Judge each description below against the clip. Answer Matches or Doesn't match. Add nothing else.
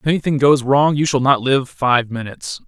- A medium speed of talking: Doesn't match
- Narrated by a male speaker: Matches